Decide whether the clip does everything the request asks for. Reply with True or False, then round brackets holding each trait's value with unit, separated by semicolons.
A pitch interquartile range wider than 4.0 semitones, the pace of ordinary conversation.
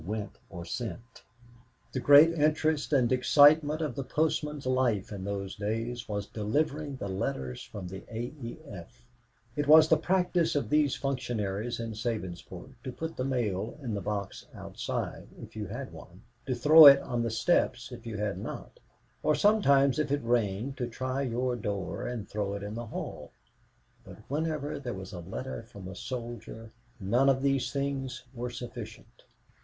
True (5.1 semitones; 170 wpm)